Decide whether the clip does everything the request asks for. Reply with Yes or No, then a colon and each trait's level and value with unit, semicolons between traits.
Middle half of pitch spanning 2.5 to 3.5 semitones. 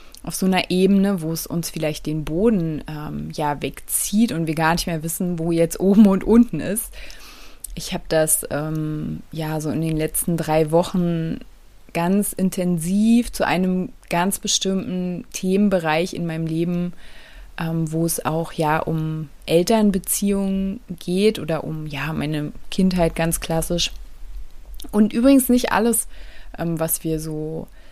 Yes: average, 3.2 semitones